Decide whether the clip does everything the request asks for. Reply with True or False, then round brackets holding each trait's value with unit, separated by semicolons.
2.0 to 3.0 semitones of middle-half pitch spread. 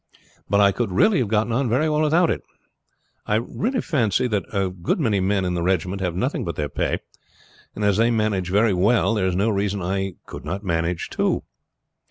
False (3.6 semitones)